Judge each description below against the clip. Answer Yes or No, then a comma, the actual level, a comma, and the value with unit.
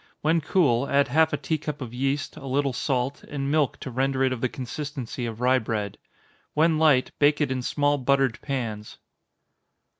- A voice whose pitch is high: No, low, 135 Hz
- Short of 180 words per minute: No, average, 185 wpm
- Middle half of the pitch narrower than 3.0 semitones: Yes, narrow, 2.6 semitones